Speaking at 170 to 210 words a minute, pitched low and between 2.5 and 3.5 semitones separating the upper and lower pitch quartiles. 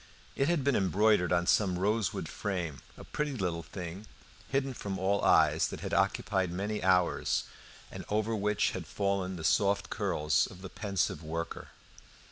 No: average, 160 wpm; very low, 95 Hz; average, 3.0 semitones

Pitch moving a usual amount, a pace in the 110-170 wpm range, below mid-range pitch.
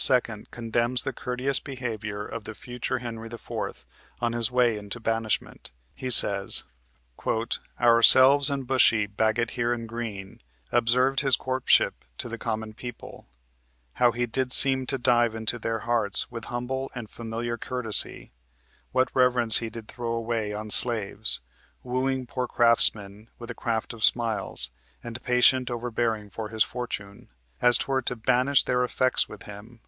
No: narrow, 2.1 semitones; average, 150 wpm; low, 120 Hz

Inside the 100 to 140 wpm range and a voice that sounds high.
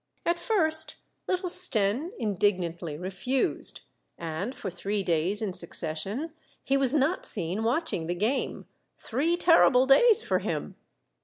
Yes: slow, 135 wpm; high, 225 Hz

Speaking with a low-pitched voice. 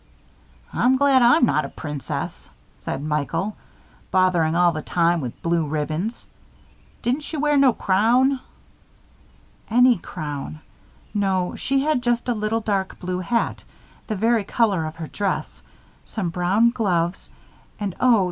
No: high, 195 Hz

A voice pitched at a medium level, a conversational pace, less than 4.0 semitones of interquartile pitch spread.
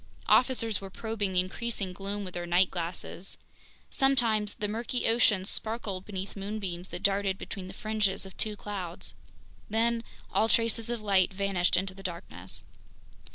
No: high, 200 Hz; average, 155 wpm; average, 2.8 semitones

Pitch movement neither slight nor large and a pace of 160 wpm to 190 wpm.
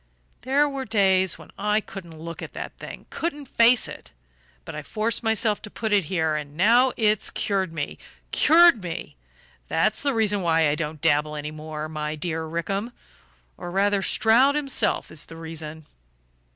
No: wide, 5.9 semitones; average, 170 wpm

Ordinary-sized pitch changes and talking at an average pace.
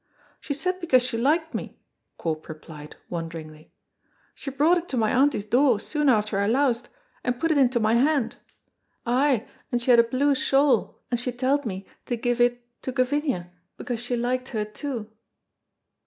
Yes: average, 4.1 semitones; average, 175 wpm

